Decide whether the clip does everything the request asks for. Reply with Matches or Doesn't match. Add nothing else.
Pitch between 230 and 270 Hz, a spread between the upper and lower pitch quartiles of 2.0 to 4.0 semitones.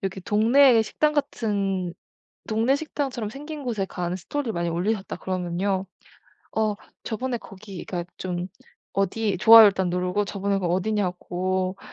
Doesn't match